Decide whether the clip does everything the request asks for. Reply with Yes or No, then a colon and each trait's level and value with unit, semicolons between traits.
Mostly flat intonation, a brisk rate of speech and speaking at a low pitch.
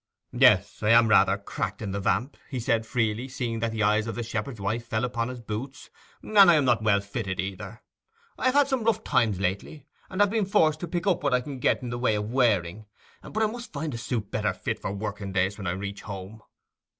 No: average, 5.1 semitones; fast, 240 wpm; low, 115 Hz